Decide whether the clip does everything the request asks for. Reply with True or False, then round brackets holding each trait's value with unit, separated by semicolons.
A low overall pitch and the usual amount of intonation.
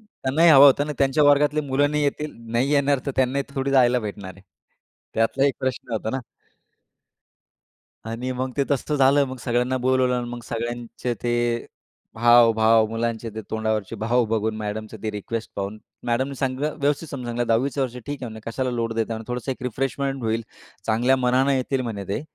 True (125 Hz; 3.2 semitones)